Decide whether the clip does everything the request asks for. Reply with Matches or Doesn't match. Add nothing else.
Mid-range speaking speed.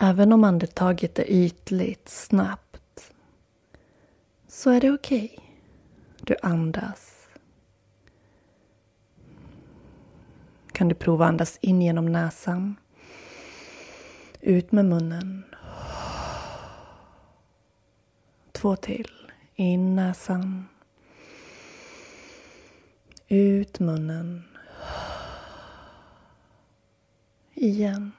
Doesn't match